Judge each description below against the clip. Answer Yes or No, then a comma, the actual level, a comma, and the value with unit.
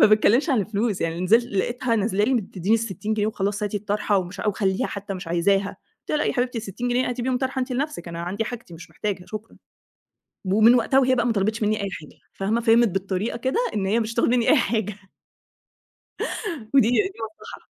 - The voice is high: Yes, high, 215 Hz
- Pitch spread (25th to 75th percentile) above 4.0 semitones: No, average, 3.6 semitones